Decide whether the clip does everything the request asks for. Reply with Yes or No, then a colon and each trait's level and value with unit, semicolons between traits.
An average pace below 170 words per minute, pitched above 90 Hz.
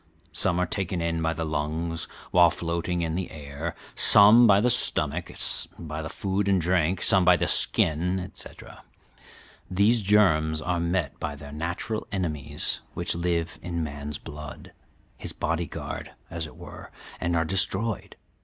No: average, 155 wpm; very low, 85 Hz